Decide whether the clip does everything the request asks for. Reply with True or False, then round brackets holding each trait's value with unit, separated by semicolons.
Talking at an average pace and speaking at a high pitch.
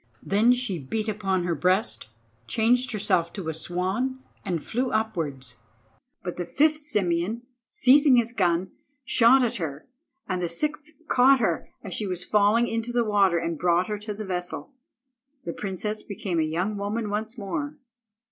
True (165 wpm; 205 Hz)